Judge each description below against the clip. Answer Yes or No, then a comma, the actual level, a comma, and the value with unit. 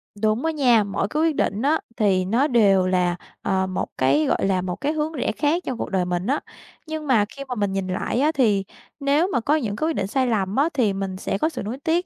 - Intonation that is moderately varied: No, wide, 7.1 semitones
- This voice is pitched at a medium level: No, high, 225 Hz